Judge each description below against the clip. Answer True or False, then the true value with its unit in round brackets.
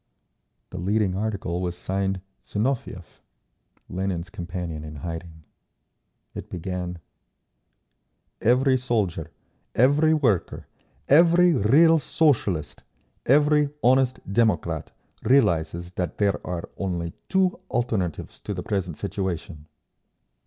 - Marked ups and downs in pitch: True (6.6 semitones)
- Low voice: True (95 Hz)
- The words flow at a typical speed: False (95 wpm)